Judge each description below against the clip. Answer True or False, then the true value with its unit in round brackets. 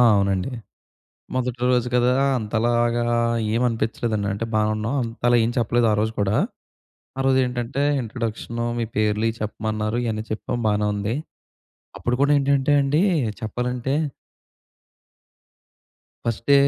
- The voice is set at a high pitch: False (115 Hz)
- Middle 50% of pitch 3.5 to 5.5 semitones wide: False (2.4 semitones)